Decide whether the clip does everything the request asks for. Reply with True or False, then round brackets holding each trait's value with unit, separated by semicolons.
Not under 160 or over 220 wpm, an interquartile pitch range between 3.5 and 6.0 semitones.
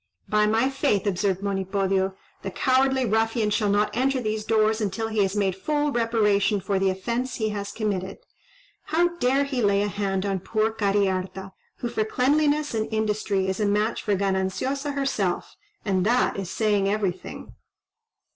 False (165 wpm; 3.1 semitones)